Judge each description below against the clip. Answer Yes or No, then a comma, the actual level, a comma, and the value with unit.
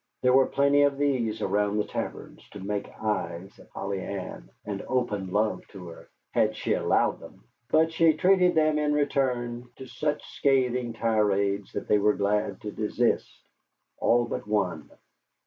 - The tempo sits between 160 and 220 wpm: Yes, average, 165 wpm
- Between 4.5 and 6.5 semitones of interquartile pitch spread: Yes, average, 5.3 semitones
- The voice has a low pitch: Yes, low, 115 Hz